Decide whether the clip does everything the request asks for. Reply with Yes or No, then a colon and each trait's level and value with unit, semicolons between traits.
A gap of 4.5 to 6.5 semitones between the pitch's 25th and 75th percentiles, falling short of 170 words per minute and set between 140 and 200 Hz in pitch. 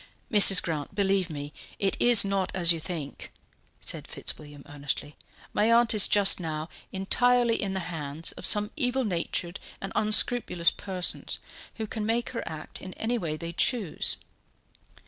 Yes: average, 5.0 semitones; average, 155 wpm; high, 190 Hz